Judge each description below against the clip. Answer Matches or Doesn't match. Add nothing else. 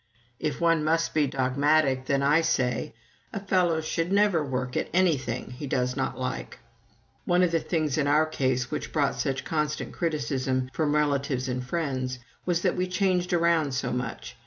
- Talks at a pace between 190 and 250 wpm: Doesn't match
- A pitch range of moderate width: Matches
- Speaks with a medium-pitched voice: Matches